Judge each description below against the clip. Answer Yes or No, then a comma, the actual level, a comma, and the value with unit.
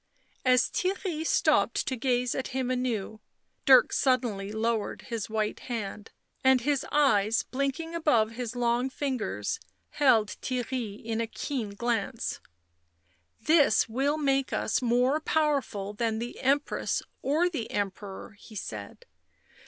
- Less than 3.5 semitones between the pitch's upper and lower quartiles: No, average, 3.9 semitones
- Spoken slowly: Yes, slow, 130 wpm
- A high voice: Yes, high, 245 Hz